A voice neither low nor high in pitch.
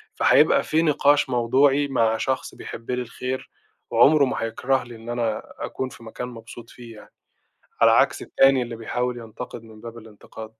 No: low, 120 Hz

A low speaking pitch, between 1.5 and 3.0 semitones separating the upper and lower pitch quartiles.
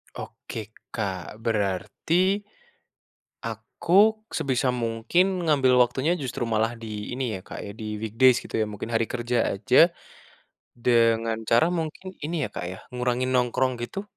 No: low, 120 Hz; average, 3.9 semitones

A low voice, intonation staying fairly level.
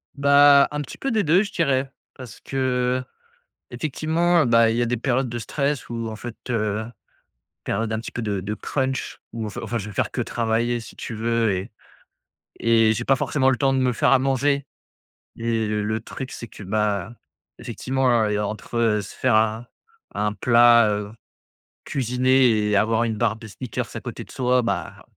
No: low, 120 Hz; average, 3.2 semitones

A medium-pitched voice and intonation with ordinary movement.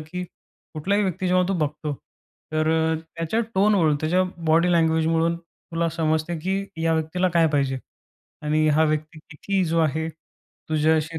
No: medium, 160 Hz; narrow, 1.9 semitones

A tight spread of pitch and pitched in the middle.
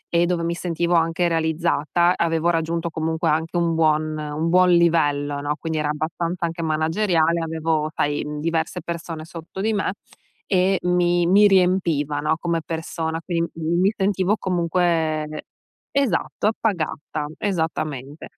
Yes: narrow, 1.9 semitones; medium, 165 Hz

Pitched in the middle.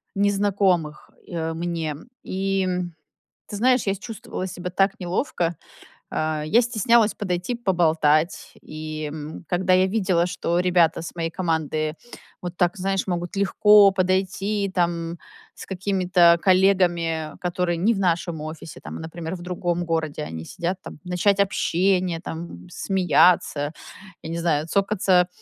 Yes: medium, 180 Hz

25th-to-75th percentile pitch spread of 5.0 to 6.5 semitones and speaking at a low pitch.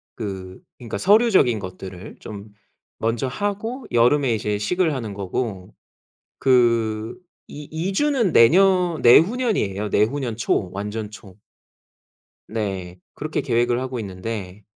No: wide, 7.1 semitones; low, 115 Hz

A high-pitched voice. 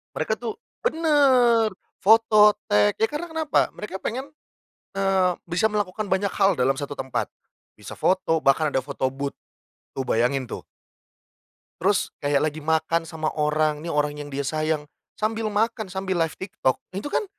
No: medium, 180 Hz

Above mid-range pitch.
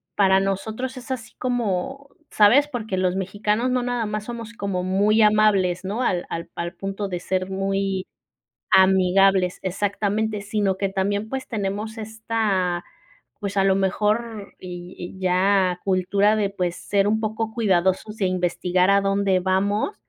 Yes: high, 200 Hz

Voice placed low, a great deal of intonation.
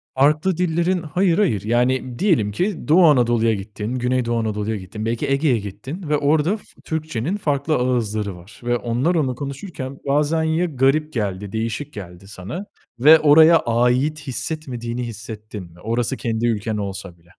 Yes: low, 125 Hz; wide, 5.9 semitones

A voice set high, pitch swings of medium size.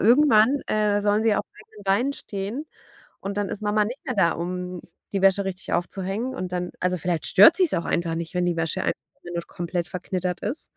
Yes: high, 195 Hz; average, 3.1 semitones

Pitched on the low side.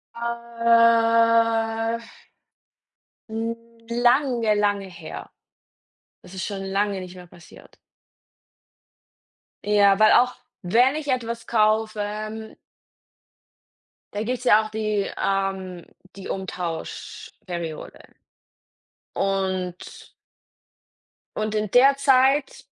No: high, 215 Hz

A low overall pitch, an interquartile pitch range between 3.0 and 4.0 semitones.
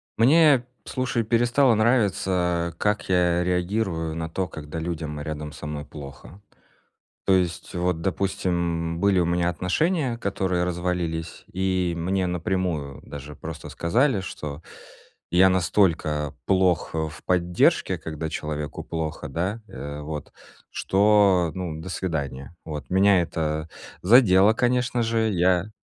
Yes: very low, 90 Hz; average, 3.3 semitones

